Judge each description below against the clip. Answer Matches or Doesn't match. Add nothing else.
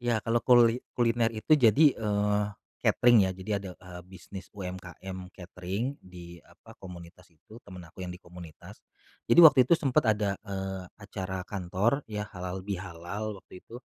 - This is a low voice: Matches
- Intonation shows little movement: Doesn't match